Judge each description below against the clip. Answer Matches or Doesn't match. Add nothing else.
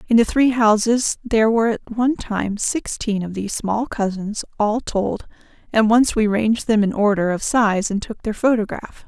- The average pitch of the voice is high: Matches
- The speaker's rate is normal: Matches